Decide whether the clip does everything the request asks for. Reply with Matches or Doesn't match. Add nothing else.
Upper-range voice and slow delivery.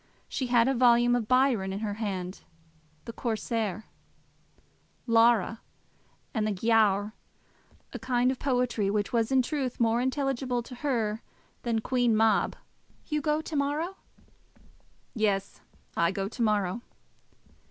Matches